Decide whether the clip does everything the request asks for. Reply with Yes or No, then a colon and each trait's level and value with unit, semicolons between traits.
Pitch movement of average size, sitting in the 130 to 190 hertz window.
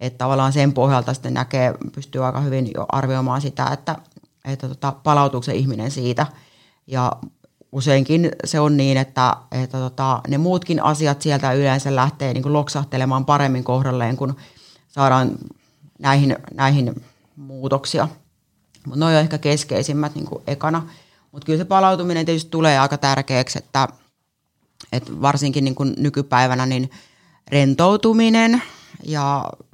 No: narrow, 2.3 semitones; medium, 140 Hz